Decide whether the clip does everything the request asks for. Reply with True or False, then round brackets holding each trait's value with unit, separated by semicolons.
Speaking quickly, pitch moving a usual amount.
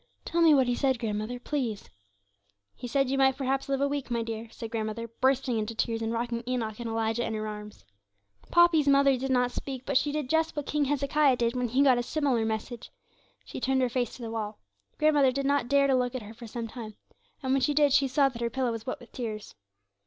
True (240 wpm; 3.2 semitones)